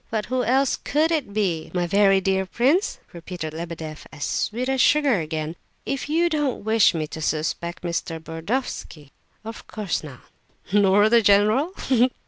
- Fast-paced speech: No, average, 170 wpm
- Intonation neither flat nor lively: No, wide, 7.5 semitones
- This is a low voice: No, high, 200 Hz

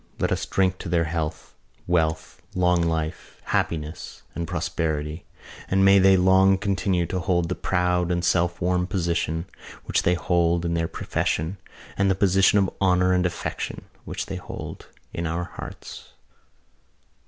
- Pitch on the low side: Yes, very low, 90 Hz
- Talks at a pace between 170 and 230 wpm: No, average, 155 wpm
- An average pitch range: No, narrow, 1.9 semitones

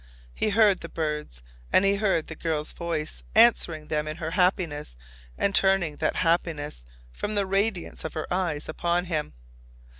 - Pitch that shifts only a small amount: No, average, 4.0 semitones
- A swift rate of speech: No, average, 160 wpm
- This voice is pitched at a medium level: Yes, medium, 170 Hz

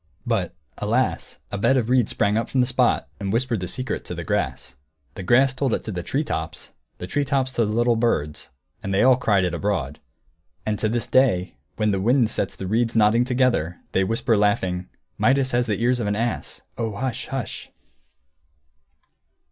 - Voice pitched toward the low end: Yes, low, 115 Hz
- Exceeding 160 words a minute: Yes, average, 195 wpm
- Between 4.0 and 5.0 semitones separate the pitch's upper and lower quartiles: Yes, average, 4.3 semitones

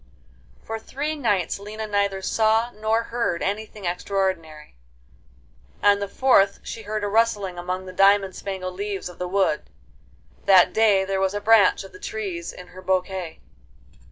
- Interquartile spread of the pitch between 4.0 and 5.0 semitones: No, narrow, 2.6 semitones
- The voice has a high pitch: Yes, high, 200 Hz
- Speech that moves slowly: No, average, 155 wpm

